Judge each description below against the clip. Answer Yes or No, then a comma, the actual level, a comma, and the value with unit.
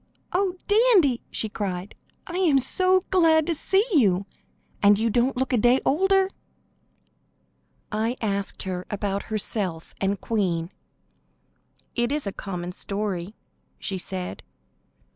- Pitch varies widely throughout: Yes, wide, 7.6 semitones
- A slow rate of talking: Yes, slow, 125 wpm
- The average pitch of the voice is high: Yes, high, 220 Hz